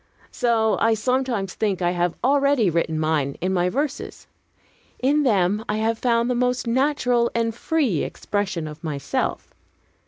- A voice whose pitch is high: Yes, high, 220 Hz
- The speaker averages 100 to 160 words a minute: Yes, average, 150 wpm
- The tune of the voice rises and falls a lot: Yes, wide, 5.9 semitones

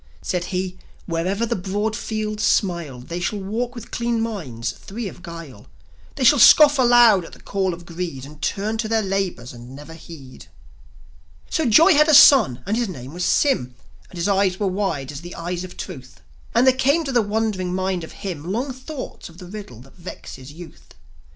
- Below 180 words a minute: No, average, 195 wpm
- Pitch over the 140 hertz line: Yes, high, 190 Hz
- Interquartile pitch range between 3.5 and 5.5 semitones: Yes, average, 5.2 semitones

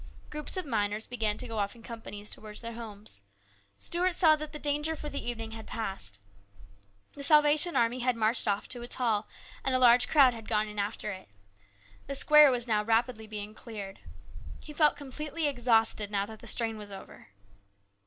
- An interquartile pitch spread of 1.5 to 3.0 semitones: No, average, 4.9 semitones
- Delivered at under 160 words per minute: No, average, 195 wpm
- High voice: Yes, high, 230 Hz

